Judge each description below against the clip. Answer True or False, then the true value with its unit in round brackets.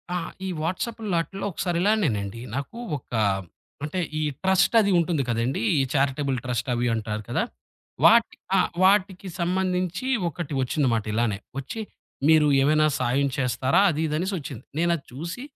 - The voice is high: False (155 Hz)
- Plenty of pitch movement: True (6.1 semitones)